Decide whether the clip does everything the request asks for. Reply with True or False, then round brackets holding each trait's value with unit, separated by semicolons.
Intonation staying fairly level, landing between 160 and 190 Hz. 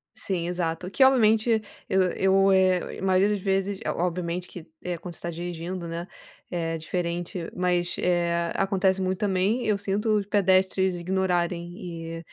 True (2.1 semitones; 185 Hz)